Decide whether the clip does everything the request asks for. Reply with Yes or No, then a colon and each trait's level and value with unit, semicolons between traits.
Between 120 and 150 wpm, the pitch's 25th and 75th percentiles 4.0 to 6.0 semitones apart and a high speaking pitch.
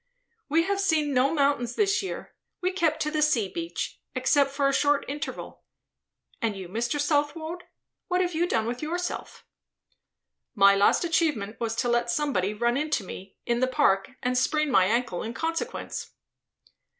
No: average, 165 wpm; wide, 5.5 semitones; very high, 280 Hz